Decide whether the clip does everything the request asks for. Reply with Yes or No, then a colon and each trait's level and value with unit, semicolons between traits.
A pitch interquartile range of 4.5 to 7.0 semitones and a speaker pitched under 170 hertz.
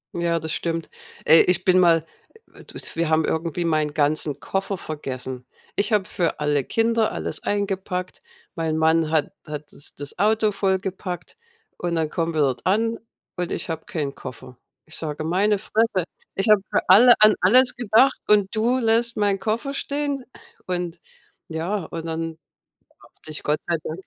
No: average, 4.8 semitones; medium, 175 Hz